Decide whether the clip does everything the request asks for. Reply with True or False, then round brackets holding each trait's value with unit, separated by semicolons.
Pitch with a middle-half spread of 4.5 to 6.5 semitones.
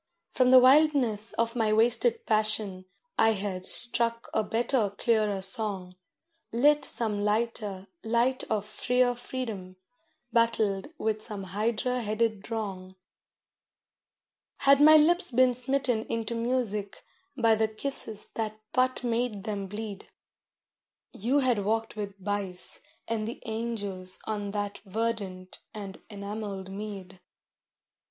False (2.8 semitones)